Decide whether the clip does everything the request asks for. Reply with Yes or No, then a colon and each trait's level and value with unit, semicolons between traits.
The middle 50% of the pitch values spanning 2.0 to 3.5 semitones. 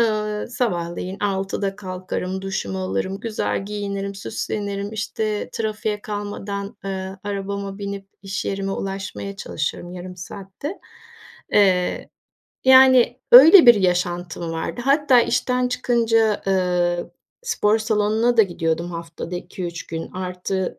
Yes: average, 3.0 semitones